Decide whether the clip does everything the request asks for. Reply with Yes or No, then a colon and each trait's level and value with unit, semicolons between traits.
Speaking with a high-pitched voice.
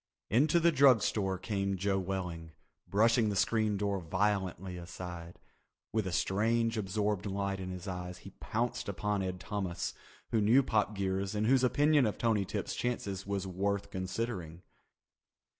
No: low, 100 Hz